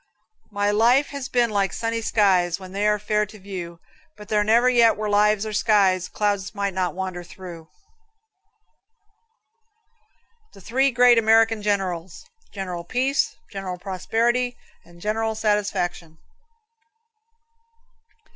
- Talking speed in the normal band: No, slow, 125 wpm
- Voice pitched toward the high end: Yes, high, 210 Hz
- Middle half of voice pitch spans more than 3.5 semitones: No, average, 3.1 semitones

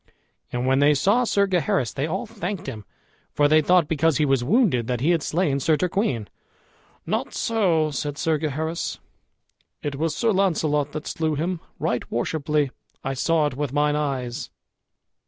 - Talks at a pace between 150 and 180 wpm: Yes, average, 170 wpm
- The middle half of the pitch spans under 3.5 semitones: No, average, 4.0 semitones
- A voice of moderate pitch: Yes, medium, 150 Hz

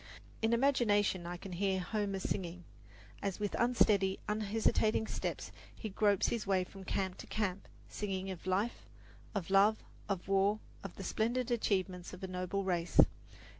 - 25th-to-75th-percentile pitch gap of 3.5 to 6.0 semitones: No, narrow, 2.4 semitones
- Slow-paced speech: No, average, 155 wpm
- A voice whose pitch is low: No, high, 195 Hz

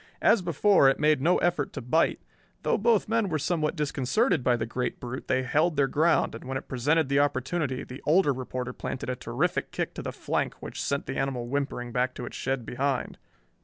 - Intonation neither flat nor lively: Yes, average, 4.1 semitones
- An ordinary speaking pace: No, fast, 210 wpm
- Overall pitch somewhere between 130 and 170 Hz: Yes, medium, 140 Hz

